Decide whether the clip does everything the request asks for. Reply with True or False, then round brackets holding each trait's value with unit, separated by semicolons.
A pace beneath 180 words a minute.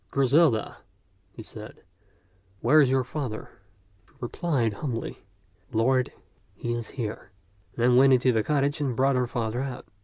True (155 wpm)